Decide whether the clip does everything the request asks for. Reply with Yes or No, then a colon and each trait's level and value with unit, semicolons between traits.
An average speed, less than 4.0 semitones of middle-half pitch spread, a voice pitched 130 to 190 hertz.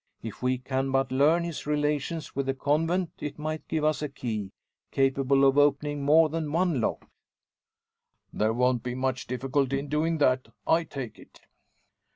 Yes: average, 170 wpm; average, 2.8 semitones; medium, 140 Hz